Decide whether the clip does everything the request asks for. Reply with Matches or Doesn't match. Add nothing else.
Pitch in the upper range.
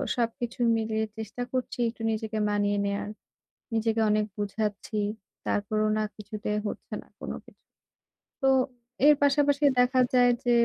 Matches